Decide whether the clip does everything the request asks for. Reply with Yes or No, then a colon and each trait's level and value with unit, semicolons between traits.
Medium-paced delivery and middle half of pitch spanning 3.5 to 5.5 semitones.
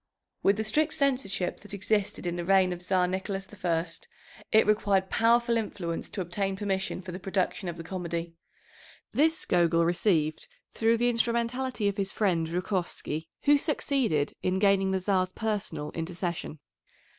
Yes: average, 155 wpm; average, 3.8 semitones